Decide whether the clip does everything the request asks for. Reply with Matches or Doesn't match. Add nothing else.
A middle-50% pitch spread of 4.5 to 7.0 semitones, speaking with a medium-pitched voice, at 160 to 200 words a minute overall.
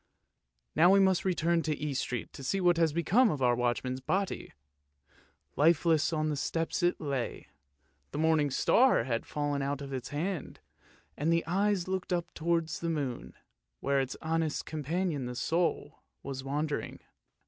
Doesn't match